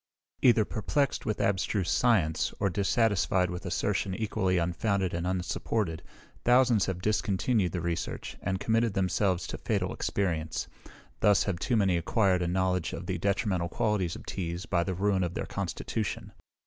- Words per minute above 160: No, average, 155 wpm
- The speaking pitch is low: Yes, very low, 95 Hz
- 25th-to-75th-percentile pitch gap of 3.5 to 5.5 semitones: No, average, 3.1 semitones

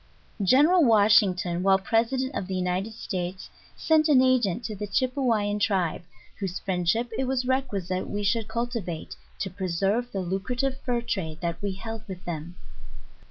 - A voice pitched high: Yes, high, 205 Hz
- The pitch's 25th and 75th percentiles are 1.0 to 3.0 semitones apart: No, average, 4.8 semitones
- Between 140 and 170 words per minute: Yes, average, 160 wpm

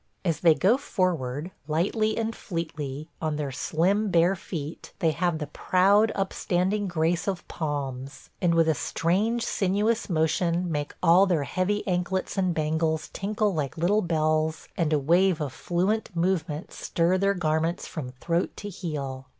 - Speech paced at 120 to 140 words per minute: No, average, 155 wpm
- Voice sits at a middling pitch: Yes, medium, 170 Hz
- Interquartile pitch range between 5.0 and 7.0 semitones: No, average, 3.5 semitones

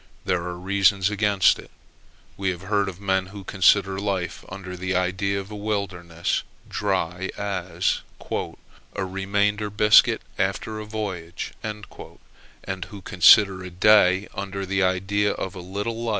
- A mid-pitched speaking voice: No, very low, 95 Hz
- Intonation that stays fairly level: Yes, narrow, 1.8 semitones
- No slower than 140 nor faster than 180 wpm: Yes, average, 145 wpm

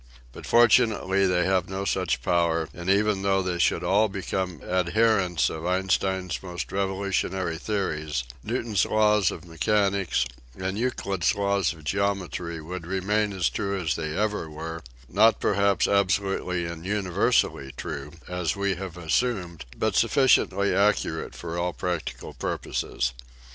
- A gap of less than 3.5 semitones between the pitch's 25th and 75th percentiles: Yes, average, 2.8 semitones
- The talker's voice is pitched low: Yes, very low, 95 Hz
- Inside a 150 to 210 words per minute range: No, average, 140 wpm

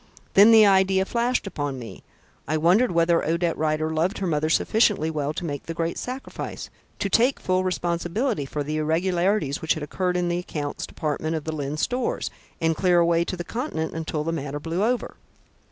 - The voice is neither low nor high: Yes, medium, 170 Hz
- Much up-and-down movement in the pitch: No, average, 3.6 semitones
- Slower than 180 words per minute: No, average, 185 wpm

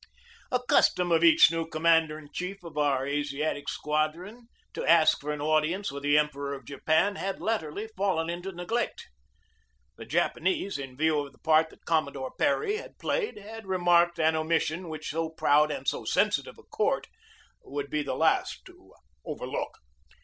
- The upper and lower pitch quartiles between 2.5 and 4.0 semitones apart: Yes, average, 3.4 semitones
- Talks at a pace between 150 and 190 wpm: Yes, average, 170 wpm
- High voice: No, medium, 160 Hz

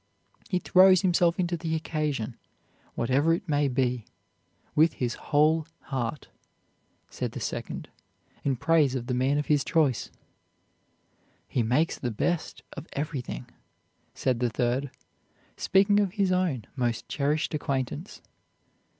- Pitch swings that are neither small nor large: Yes, average, 4.6 semitones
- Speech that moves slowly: Yes, slow, 130 wpm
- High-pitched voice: No, medium, 145 Hz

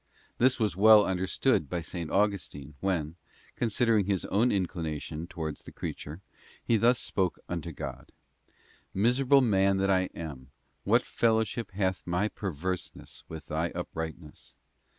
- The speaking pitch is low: Yes, very low, 95 Hz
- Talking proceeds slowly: Yes, slow, 130 wpm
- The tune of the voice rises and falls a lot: No, average, 4.7 semitones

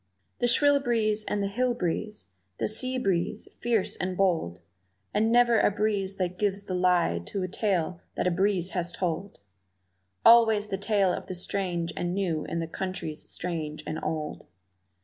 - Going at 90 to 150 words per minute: No, average, 170 wpm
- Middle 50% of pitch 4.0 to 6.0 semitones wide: No, average, 3.6 semitones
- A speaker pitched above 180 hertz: Yes, high, 190 Hz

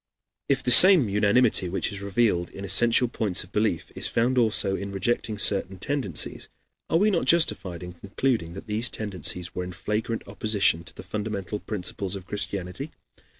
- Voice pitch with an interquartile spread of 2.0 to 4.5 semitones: Yes, average, 3.9 semitones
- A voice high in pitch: No, low, 100 Hz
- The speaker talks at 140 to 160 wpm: No, average, 170 wpm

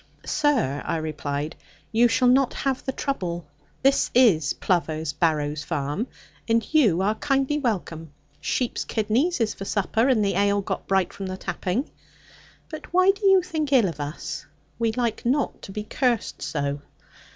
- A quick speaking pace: No, average, 160 wpm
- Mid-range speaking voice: No, high, 215 Hz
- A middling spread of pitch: No, wide, 8.1 semitones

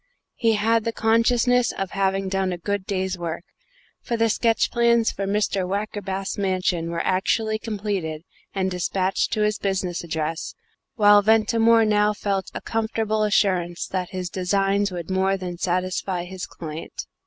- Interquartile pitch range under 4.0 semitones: Yes, average, 2.8 semitones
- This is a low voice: No, high, 195 Hz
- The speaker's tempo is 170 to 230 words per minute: No, average, 155 wpm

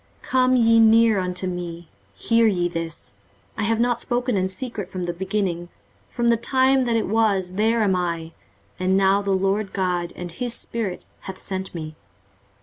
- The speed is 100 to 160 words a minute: No, average, 180 wpm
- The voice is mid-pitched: No, high, 195 Hz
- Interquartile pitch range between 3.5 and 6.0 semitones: Yes, average, 4.2 semitones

